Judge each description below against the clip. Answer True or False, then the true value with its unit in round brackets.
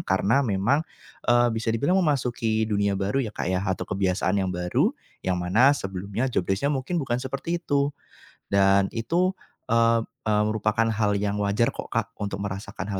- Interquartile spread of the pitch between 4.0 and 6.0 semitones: True (4.4 semitones)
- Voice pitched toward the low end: True (110 Hz)